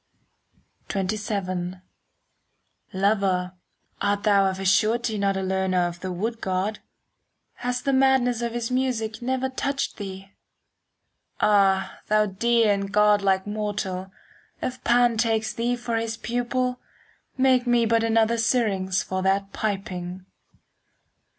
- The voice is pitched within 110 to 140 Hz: No, high, 210 Hz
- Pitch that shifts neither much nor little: Yes, average, 3.7 semitones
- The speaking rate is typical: No, slow, 125 wpm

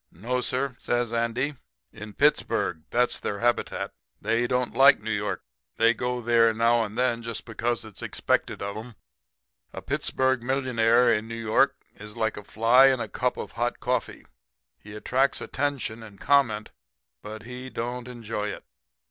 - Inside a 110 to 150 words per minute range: No, average, 165 wpm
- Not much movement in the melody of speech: Yes, narrow, 2.3 semitones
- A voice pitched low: Yes, low, 115 Hz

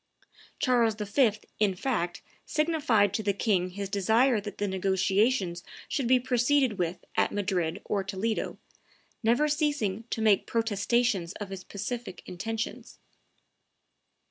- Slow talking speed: Yes, slow, 125 wpm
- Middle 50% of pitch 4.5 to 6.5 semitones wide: No, average, 4.0 semitones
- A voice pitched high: Yes, high, 210 Hz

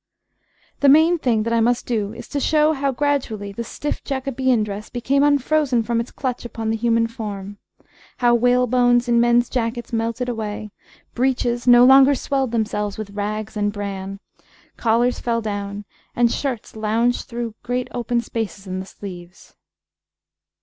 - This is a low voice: No, high, 235 Hz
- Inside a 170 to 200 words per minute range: No, average, 155 wpm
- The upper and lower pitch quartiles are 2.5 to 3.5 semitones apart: Yes, average, 2.8 semitones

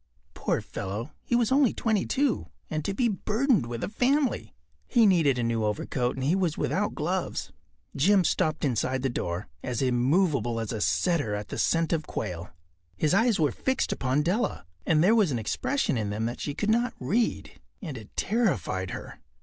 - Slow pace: No, average, 185 wpm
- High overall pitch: No, medium, 150 Hz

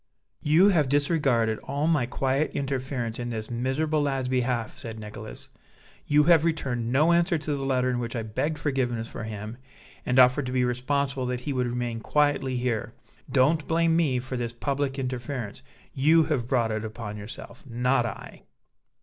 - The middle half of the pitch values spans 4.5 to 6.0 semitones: No, average, 3.4 semitones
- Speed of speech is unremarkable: Yes, average, 175 wpm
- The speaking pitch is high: No, low, 130 Hz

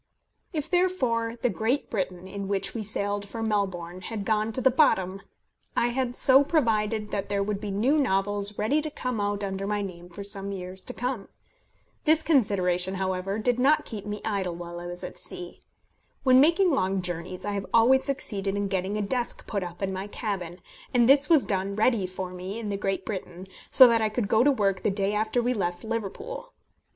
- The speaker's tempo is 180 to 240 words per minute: Yes, fast, 205 wpm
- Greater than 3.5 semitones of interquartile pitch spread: Yes, average, 4.0 semitones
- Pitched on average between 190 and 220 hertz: Yes, high, 205 Hz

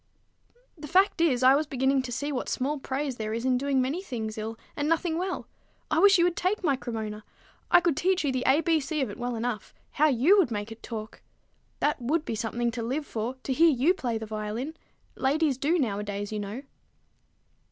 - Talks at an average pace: No, fast, 215 wpm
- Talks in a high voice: Yes, very high, 265 Hz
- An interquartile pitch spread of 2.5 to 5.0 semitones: No, wide, 5.4 semitones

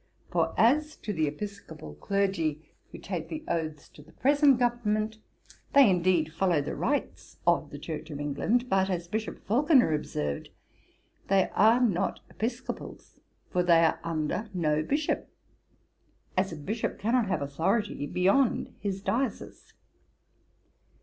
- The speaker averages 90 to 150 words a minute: Yes, slow, 135 wpm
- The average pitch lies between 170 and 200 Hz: Yes, high, 190 Hz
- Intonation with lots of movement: Yes, wide, 6.4 semitones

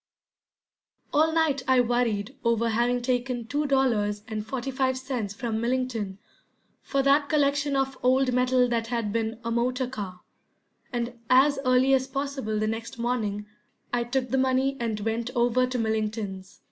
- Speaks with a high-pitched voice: Yes, high, 245 Hz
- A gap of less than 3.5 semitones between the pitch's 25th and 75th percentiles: Yes, average, 2.8 semitones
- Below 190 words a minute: Yes, average, 160 wpm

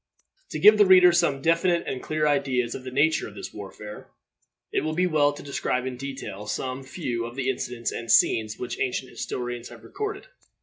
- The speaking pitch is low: Yes, low, 130 Hz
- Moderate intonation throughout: Yes, average, 4.4 semitones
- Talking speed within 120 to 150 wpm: No, average, 200 wpm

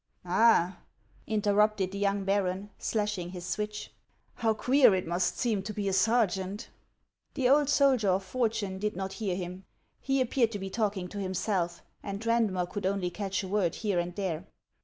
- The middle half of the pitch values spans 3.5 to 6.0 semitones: No, average, 2.7 semitones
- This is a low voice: No, high, 200 Hz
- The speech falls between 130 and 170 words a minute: No, average, 180 wpm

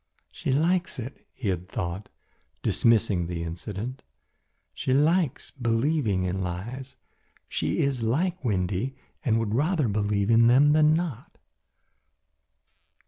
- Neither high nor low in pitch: No, low, 115 Hz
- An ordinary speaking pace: No, slow, 120 wpm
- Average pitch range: No, wide, 6.2 semitones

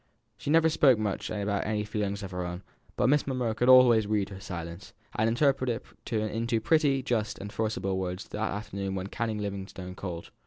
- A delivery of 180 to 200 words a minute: Yes, average, 190 wpm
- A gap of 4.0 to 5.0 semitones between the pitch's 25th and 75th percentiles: No, average, 3.5 semitones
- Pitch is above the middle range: No, low, 105 Hz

